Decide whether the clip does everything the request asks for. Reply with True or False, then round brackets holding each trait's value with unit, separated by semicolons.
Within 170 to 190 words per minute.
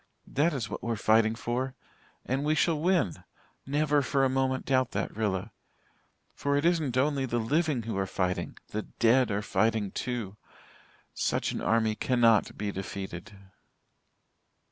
False (150 wpm)